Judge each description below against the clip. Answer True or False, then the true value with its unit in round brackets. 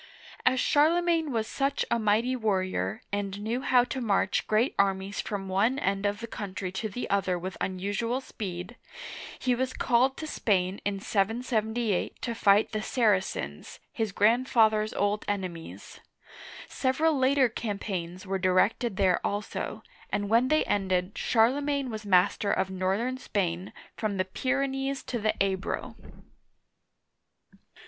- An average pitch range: True (4.4 semitones)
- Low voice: False (215 Hz)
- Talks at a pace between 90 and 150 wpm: True (140 wpm)